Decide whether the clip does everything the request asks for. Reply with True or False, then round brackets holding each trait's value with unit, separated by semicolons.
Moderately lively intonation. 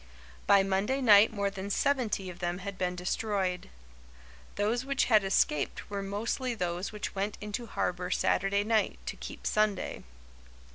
False (2.2 semitones)